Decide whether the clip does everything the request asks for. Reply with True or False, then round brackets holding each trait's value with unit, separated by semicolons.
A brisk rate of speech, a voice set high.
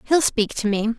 True (245 wpm; 235 Hz)